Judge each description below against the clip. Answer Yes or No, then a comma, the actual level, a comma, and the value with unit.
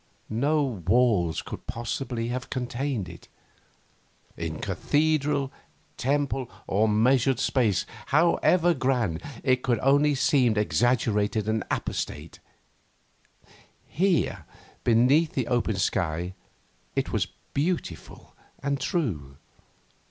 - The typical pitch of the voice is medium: No, low, 125 Hz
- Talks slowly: Yes, slow, 100 wpm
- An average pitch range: Yes, average, 4.8 semitones